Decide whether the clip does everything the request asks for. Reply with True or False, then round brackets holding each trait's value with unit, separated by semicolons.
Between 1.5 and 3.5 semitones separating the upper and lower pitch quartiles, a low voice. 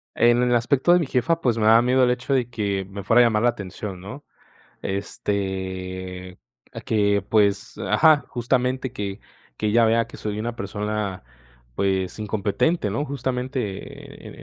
False (3.9 semitones; 110 Hz)